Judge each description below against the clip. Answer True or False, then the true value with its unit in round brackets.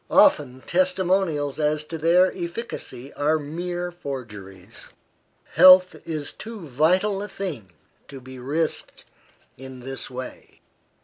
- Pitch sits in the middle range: True (155 Hz)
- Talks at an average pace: False (115 wpm)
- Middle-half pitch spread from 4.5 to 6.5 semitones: True (5.4 semitones)